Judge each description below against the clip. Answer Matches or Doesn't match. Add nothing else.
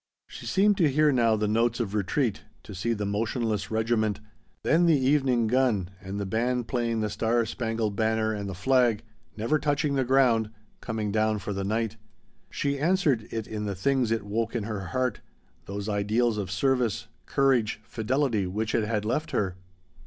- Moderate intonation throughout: Matches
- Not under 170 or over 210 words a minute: Matches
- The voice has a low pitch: Matches